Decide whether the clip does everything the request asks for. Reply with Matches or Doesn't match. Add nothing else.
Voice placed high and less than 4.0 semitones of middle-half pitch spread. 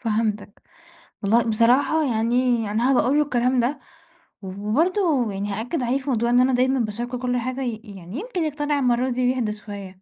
Matches